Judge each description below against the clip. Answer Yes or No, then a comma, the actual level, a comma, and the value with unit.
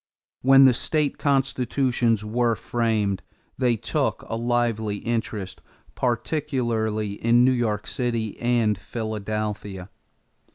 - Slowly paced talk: Yes, slow, 100 wpm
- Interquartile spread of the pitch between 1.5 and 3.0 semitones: Yes, narrow, 2.5 semitones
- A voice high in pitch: No, low, 115 Hz